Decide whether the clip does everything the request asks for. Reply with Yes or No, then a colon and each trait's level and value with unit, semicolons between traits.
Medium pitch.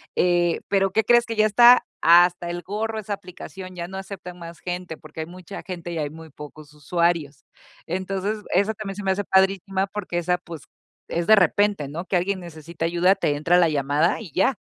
Yes: medium, 180 Hz